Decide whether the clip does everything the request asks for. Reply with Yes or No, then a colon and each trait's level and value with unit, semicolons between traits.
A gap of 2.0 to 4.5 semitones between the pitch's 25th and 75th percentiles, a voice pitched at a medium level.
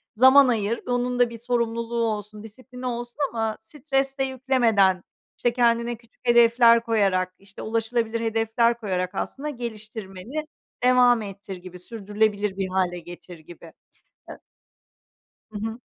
No: average, 3.2 semitones; high, 230 Hz